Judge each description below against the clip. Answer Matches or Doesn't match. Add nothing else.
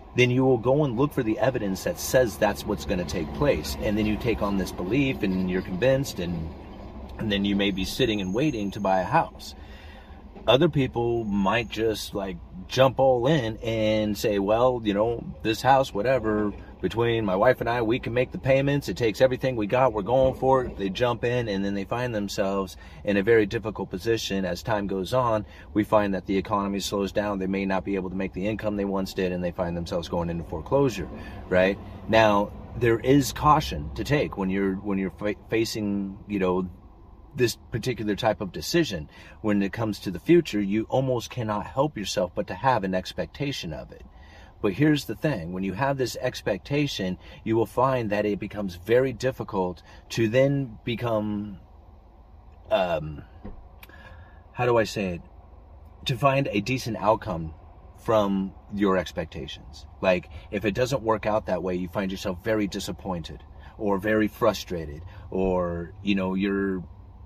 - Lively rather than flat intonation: Doesn't match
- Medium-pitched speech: Doesn't match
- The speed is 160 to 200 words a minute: Matches